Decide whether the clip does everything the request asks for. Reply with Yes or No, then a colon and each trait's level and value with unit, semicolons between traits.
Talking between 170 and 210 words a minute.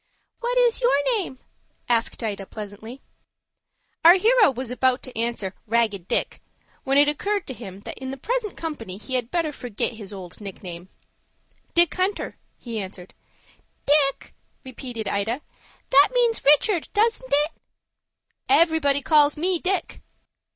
No: average, 140 wpm